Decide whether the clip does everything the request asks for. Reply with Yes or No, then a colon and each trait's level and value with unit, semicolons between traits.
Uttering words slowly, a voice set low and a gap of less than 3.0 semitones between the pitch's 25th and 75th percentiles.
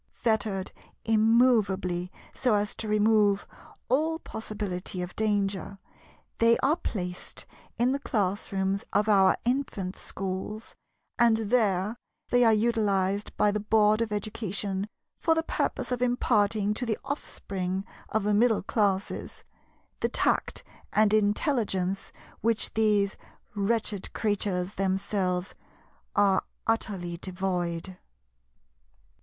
No: slow, 110 wpm; high, 205 Hz; narrow, 2.6 semitones